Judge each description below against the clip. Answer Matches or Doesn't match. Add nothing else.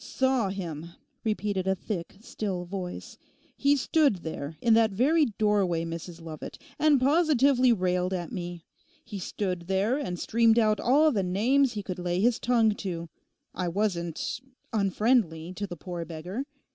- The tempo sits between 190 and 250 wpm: Doesn't match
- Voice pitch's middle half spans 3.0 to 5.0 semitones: Doesn't match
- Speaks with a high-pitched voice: Matches